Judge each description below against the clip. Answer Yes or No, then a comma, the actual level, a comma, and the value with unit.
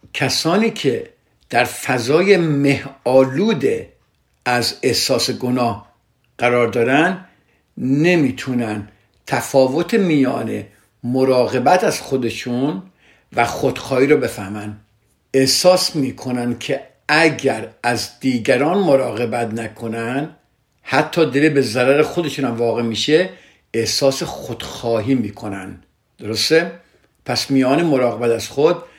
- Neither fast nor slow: No, slow, 95 wpm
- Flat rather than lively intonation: No, average, 4.5 semitones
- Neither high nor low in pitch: No, low, 130 Hz